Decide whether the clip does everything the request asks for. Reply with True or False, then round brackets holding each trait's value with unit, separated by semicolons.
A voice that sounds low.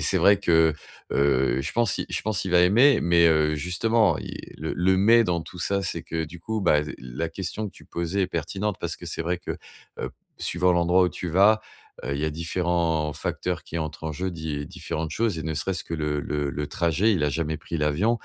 True (85 Hz)